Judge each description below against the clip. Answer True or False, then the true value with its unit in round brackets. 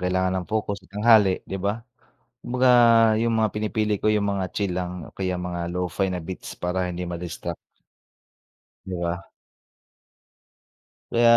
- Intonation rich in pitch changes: False (3.0 semitones)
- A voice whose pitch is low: True (95 Hz)